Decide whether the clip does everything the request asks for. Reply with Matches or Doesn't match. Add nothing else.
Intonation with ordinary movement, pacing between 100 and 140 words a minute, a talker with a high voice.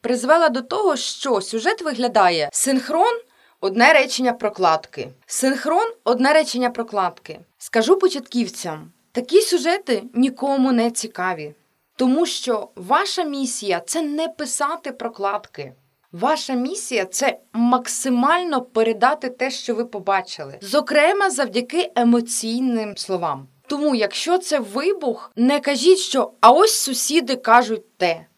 Doesn't match